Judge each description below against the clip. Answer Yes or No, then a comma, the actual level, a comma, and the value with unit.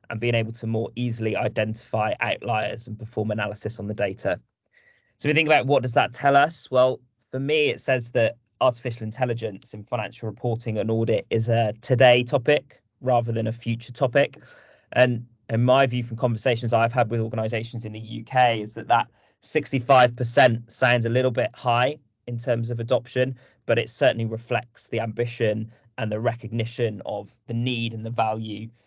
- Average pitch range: No, narrow, 2.0 semitones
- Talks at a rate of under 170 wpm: No, average, 180 wpm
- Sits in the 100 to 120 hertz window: Yes, low, 115 Hz